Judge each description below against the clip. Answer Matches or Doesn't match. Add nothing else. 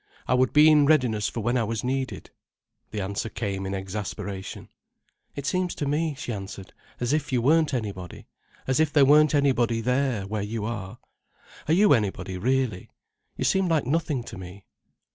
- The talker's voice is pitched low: Matches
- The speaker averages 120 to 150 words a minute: Doesn't match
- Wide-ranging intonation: Matches